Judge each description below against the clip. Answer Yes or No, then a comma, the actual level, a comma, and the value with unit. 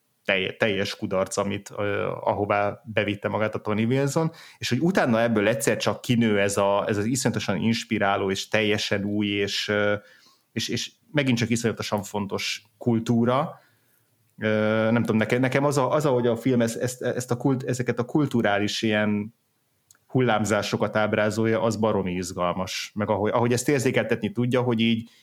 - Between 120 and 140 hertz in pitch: No, low, 110 Hz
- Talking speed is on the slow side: No, average, 150 wpm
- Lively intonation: No, narrow, 2.6 semitones